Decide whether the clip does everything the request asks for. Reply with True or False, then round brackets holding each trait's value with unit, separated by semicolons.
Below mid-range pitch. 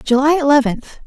False (275 Hz)